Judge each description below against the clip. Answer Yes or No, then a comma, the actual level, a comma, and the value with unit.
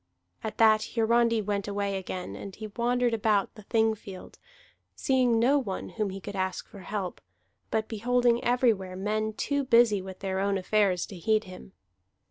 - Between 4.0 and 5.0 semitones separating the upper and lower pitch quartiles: No, average, 3.1 semitones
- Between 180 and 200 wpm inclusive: No, average, 170 wpm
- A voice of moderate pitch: No, high, 215 Hz